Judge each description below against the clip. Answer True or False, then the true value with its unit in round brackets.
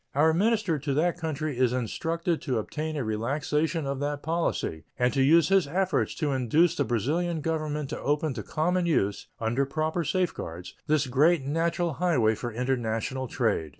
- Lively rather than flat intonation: False (4.5 semitones)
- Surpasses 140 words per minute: True (170 wpm)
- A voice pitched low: False (150 Hz)